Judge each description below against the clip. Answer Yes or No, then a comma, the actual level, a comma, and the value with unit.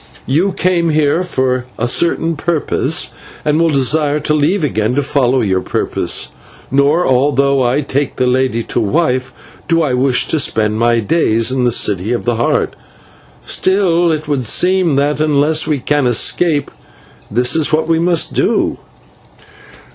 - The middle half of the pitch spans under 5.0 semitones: Yes, average, 4.3 semitones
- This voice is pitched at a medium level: Yes, medium, 145 Hz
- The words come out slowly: No, average, 160 wpm